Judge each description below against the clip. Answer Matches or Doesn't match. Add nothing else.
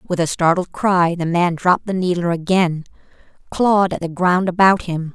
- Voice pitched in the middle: Matches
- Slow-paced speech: Doesn't match